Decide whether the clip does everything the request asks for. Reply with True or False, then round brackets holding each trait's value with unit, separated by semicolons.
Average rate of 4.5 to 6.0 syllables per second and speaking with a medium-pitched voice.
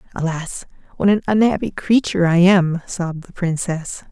True (5.0 syllables/s; 180 Hz)